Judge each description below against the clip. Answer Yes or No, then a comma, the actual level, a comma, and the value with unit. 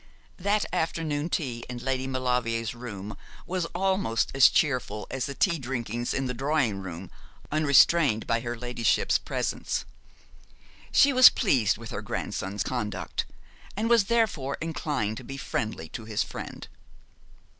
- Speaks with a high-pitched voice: No, low, 130 Hz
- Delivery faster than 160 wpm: No, average, 140 wpm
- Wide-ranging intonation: Yes, wide, 5.7 semitones